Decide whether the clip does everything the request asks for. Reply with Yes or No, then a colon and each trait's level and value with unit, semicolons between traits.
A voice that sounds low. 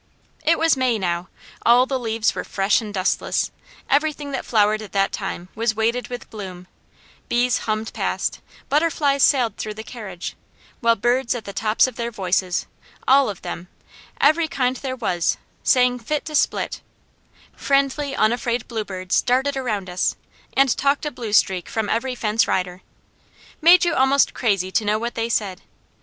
No: high, 230 Hz